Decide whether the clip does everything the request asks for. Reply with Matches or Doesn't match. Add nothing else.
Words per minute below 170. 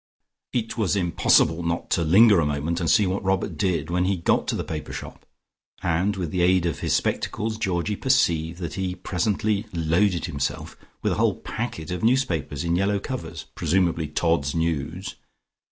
Doesn't match